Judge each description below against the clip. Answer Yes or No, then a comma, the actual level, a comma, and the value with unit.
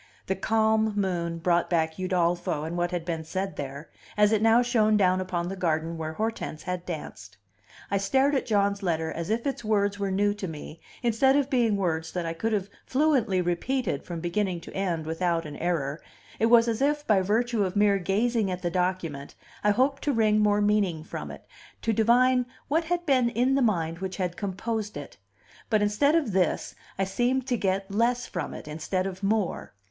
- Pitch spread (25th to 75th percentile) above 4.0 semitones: Yes, average, 4.6 semitones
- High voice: Yes, high, 195 Hz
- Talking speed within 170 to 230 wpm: Yes, average, 200 wpm